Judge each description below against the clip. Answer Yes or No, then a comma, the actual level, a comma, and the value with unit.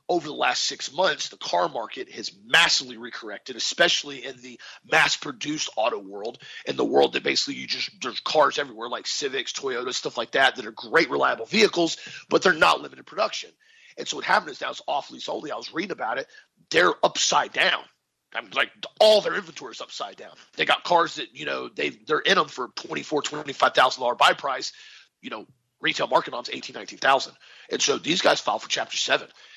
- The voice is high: Yes, very high, 390 Hz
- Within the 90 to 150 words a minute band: No, average, 200 wpm